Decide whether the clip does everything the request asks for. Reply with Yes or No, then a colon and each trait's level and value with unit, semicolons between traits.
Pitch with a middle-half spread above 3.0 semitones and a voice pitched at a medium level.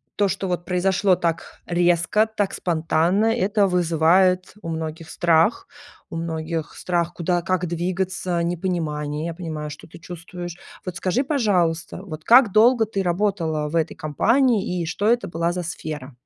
No: average, 2.7 semitones; medium, 175 Hz